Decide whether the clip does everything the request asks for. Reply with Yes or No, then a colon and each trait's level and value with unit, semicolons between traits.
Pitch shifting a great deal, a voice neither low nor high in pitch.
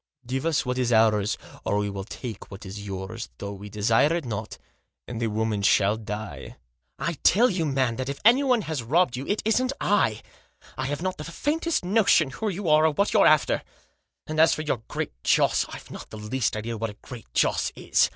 No: wide, 7.6 semitones; low, 130 Hz